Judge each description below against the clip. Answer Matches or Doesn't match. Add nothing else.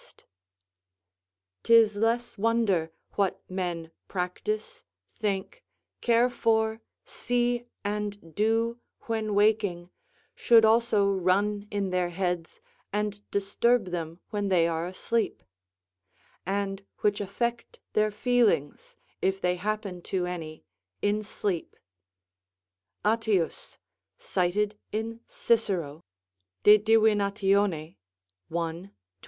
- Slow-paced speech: Matches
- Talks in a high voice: Matches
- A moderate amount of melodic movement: Matches